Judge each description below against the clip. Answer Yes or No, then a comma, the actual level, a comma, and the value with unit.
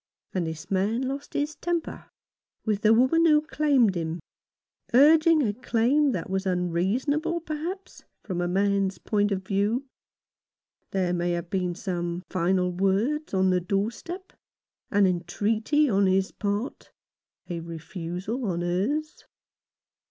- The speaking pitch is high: Yes, high, 200 Hz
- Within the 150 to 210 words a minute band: No, average, 140 wpm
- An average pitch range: No, wide, 7.5 semitones